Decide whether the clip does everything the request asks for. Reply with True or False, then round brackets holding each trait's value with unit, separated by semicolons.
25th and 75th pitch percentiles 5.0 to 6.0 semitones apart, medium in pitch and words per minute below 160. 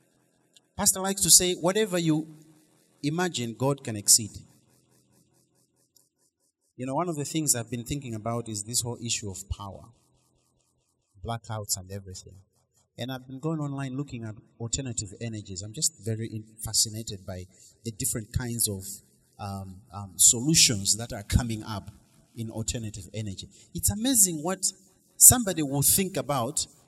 False (5.6 semitones; 115 Hz; 145 wpm)